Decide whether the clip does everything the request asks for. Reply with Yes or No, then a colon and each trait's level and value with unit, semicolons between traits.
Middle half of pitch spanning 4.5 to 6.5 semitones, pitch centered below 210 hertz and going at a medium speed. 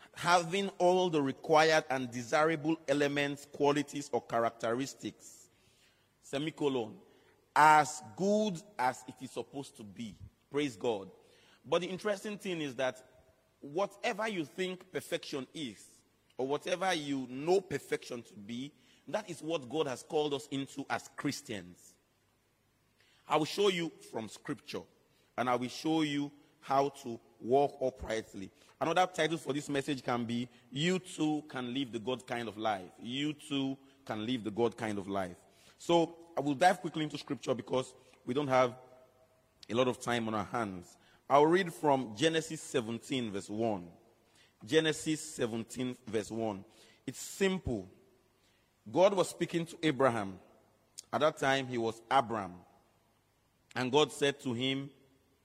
Yes: average, 4.8 semitones; low, 135 Hz; average, 145 wpm